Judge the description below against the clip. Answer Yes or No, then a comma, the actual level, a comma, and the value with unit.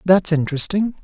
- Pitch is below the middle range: No, medium, 180 Hz